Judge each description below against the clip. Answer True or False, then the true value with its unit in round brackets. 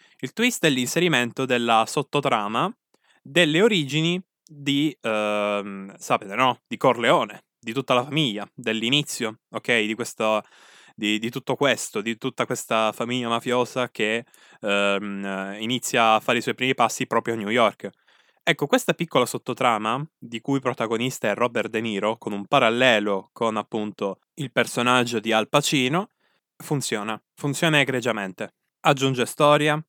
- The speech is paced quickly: False (145 wpm)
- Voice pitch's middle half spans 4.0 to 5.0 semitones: True (4.3 semitones)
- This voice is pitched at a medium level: False (120 Hz)